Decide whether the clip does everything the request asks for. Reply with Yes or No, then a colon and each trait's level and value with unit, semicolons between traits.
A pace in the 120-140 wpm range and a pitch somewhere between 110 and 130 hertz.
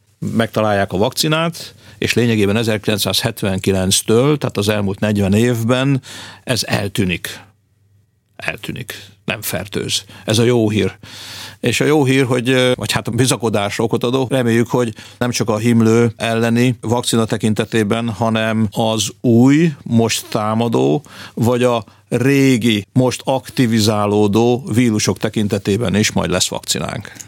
Yes: average, 125 wpm; low, 115 Hz